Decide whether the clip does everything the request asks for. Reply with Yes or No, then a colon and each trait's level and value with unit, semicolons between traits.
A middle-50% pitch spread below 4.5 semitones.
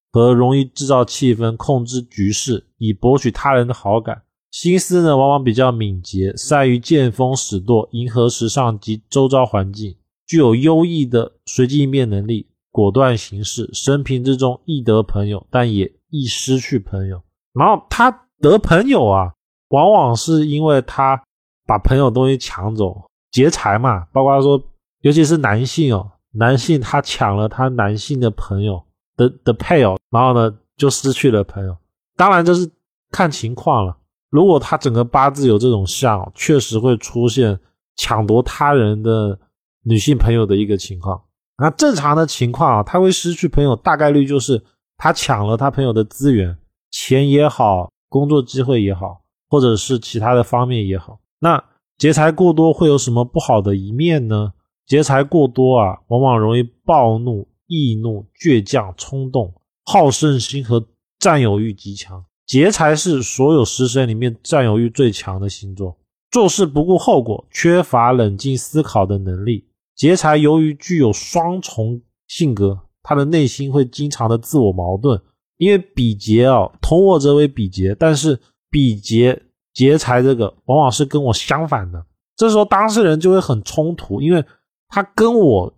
No: average, 5.3 semitones